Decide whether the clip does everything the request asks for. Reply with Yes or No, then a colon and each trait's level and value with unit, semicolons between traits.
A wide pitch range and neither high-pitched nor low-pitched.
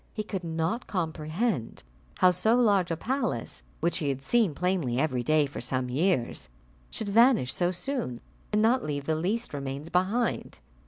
Yes: wide, 7.1 semitones; medium, 175 Hz